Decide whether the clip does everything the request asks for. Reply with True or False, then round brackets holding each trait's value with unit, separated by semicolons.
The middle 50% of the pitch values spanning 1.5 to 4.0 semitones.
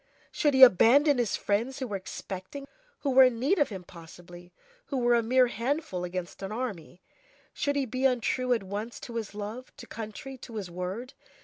False (5.2 semitones)